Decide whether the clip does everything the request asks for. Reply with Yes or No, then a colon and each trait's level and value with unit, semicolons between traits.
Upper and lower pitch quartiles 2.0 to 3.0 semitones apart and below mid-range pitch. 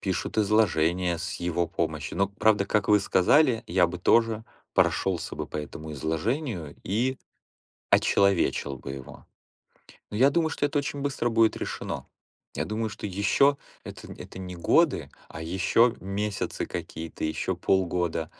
No: average, 4.8 semitones; low, 100 Hz